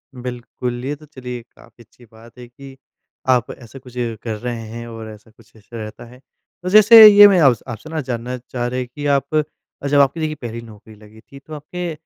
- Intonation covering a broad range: No, average, 3.6 semitones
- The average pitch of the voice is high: No, low, 125 Hz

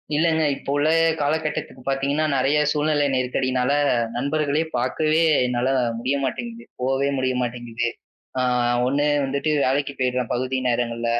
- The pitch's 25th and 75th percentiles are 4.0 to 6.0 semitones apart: No, average, 3.0 semitones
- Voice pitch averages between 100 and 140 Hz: Yes, low, 135 Hz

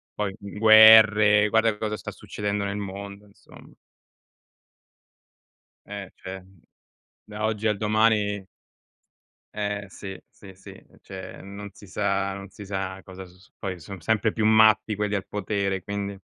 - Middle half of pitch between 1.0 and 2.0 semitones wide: Yes, narrow, 1.5 semitones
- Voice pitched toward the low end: Yes, low, 100 Hz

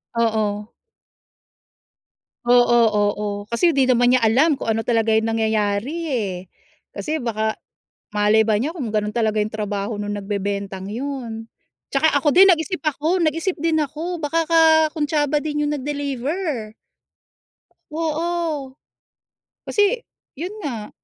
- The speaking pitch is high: Yes, very high, 255 Hz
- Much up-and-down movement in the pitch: Yes, wide, 6.4 semitones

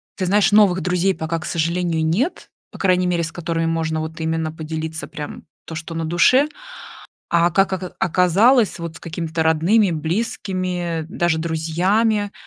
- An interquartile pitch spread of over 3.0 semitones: No, average, 2.7 semitones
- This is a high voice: No, medium, 170 Hz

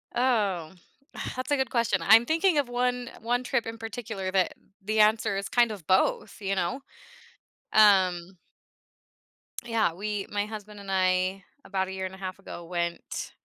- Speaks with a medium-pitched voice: No, high, 205 Hz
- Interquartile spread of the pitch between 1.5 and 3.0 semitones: No, average, 3.7 semitones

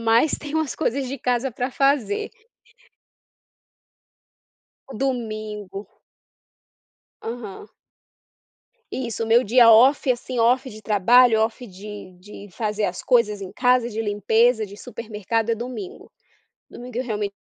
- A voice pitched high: Yes, high, 230 Hz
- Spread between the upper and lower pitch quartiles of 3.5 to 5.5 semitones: No, average, 3.1 semitones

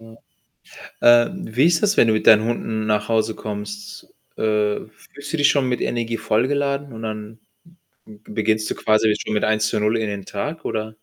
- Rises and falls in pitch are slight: Yes, narrow, 2.2 semitones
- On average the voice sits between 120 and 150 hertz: No, low, 110 Hz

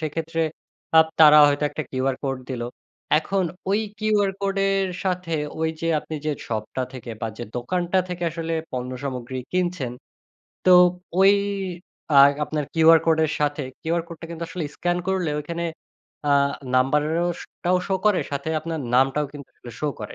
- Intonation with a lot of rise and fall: No, average, 4.2 semitones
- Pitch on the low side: No, medium, 160 Hz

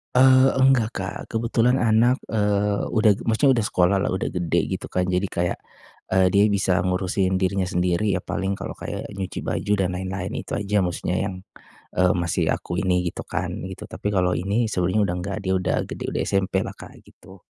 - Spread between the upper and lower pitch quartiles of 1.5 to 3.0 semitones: Yes, average, 2.7 semitones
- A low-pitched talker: Yes, very low, 95 Hz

